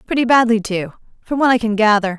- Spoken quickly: Yes, fast, 220 wpm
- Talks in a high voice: Yes, high, 225 Hz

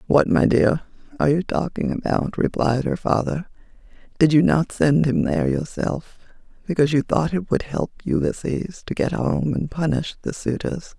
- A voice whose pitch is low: No, medium, 155 Hz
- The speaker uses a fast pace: No, average, 170 wpm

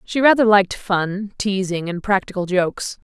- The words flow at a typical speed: Yes, average, 155 wpm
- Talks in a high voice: Yes, high, 195 Hz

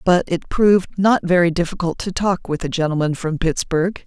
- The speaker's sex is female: Yes, female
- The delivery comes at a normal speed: Yes, average, 190 wpm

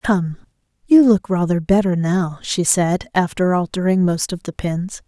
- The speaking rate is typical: Yes, average, 165 wpm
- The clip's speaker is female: Yes, female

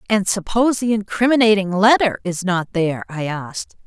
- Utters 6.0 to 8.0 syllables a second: No, 5.4 syllables/s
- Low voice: No, high, 200 Hz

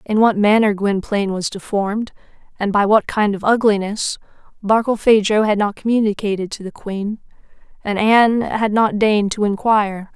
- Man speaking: No, female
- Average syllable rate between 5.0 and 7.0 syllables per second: Yes, 5.2 syllables/s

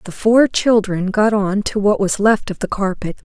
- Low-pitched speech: No, high, 205 Hz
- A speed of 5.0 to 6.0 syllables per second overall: No, 4.5 syllables/s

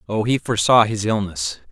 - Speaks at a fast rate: No, average, 175 wpm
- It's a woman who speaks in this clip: No, male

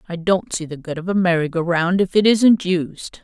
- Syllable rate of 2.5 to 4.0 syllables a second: No, 4.9 syllables/s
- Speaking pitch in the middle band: Yes, medium, 175 Hz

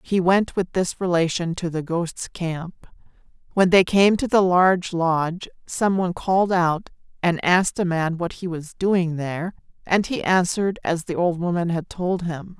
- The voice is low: No, medium, 175 Hz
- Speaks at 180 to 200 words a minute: Yes, average, 185 wpm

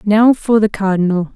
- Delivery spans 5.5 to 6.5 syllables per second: No, 4.8 syllables/s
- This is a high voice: Yes, high, 205 Hz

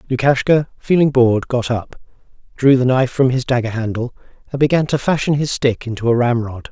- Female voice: No, male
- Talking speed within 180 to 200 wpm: Yes, average, 190 wpm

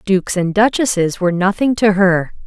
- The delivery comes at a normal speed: Yes, average, 170 wpm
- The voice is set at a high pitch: Yes, high, 195 Hz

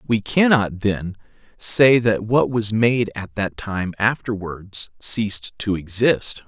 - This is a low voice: Yes, low, 105 Hz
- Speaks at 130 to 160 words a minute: Yes, average, 140 wpm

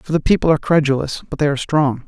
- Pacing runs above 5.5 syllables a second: Yes, 7.1 syllables/s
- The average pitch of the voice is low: No, medium, 145 Hz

